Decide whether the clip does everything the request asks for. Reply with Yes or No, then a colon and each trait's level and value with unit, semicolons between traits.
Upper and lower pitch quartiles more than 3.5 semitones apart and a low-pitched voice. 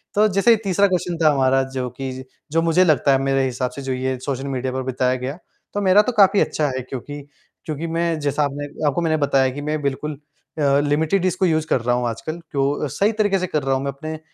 No: average, 3.9 semitones; medium, 145 Hz